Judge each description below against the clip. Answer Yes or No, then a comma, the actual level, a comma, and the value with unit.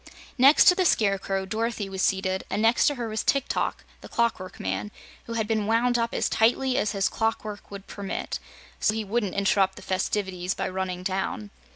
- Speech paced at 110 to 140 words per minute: No, average, 195 wpm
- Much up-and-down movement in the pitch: No, average, 3.3 semitones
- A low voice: No, high, 205 Hz